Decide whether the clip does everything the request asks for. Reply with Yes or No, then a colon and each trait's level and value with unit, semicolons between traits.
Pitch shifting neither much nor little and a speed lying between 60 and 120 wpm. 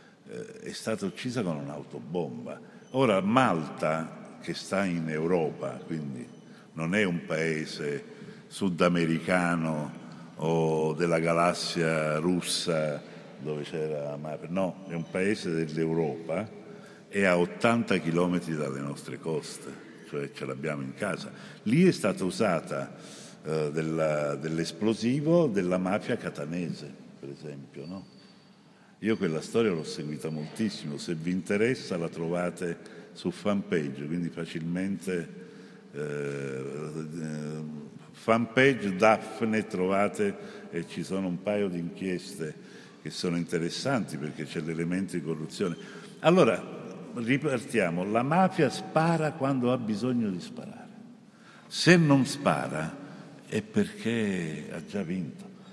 No: wide, 5.8 semitones; slow, 115 wpm